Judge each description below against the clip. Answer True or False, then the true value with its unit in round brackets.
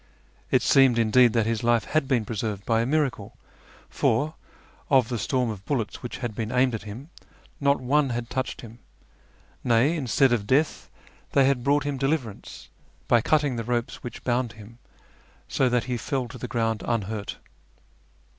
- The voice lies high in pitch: False (120 Hz)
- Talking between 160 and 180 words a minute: True (175 wpm)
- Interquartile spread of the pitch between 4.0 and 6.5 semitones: False (3.0 semitones)